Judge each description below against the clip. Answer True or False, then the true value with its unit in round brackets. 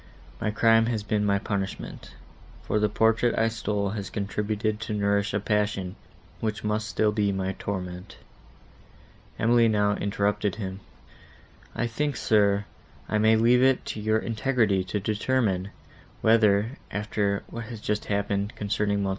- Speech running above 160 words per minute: False (145 wpm)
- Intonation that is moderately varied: False (1.8 semitones)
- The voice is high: False (105 Hz)